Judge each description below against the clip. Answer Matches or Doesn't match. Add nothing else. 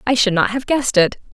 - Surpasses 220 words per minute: Matches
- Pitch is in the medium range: Doesn't match